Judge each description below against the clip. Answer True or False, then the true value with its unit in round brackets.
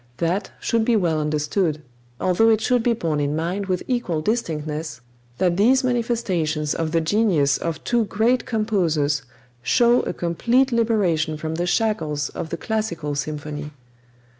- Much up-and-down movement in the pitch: True (6.5 semitones)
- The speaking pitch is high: False (175 Hz)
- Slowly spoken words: False (150 wpm)